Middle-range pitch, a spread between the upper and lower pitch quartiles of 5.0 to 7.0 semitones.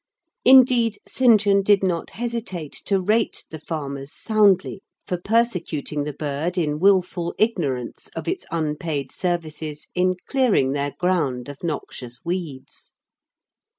Yes: medium, 175 Hz; average, 5.3 semitones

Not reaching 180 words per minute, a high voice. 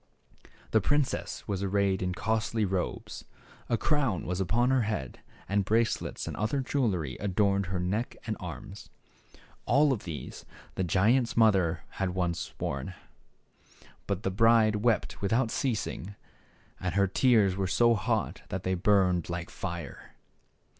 No: average, 140 wpm; low, 100 Hz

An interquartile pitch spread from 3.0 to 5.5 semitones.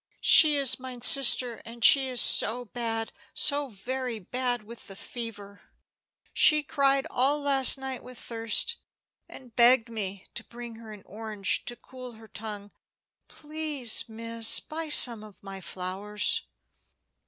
Yes: average, 3.3 semitones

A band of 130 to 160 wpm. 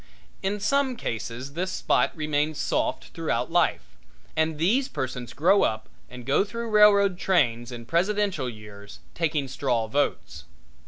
Yes: average, 140 wpm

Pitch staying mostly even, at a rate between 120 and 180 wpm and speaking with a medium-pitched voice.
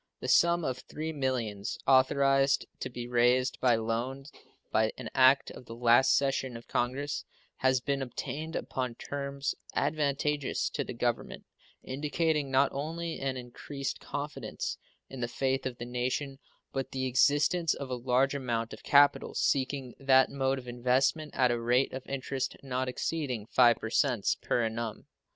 No: narrow, 2.3 semitones; average, 155 wpm; low, 130 Hz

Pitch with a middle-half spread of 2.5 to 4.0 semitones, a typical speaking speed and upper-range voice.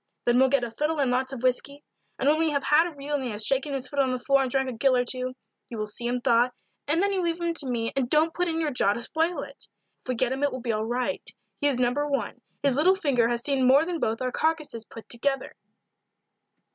No: average, 3.3 semitones; fast, 275 wpm; very high, 270 Hz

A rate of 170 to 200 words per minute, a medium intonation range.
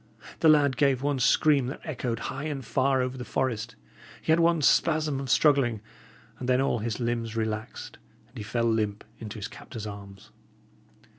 Yes: average, 175 wpm; average, 3.8 semitones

